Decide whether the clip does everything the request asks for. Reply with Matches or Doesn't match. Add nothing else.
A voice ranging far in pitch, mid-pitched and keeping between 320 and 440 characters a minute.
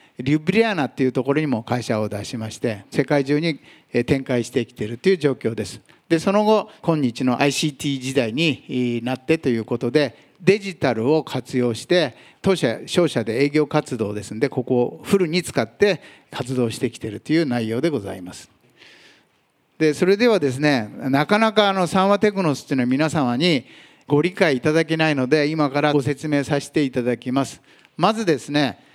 Doesn't match